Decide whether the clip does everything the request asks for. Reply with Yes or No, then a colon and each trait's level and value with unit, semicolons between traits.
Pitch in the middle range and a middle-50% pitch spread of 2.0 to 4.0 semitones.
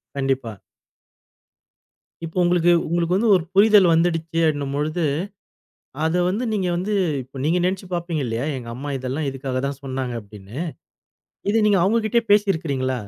No: medium, 160 Hz; wide, 5.4 semitones